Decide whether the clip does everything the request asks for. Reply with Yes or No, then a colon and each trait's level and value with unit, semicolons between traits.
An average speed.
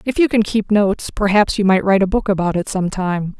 No: fast, 265 wpm